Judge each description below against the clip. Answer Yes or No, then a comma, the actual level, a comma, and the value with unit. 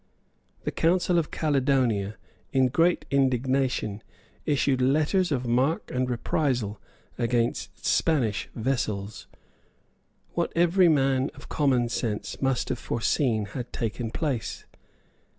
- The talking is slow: Yes, slow, 110 wpm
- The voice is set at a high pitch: No, low, 130 Hz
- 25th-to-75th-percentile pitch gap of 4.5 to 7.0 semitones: No, average, 3.8 semitones